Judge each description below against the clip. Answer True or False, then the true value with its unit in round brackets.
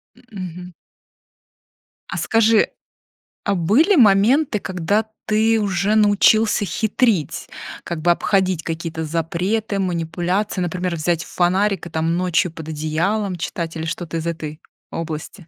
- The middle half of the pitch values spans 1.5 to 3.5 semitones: False (4.1 semitones)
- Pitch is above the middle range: False (180 Hz)